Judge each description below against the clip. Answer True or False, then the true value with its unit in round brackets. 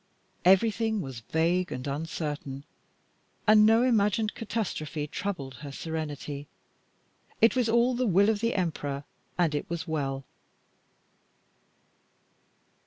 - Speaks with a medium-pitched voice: True (170 Hz)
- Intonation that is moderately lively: False (6.9 semitones)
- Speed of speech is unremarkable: False (110 wpm)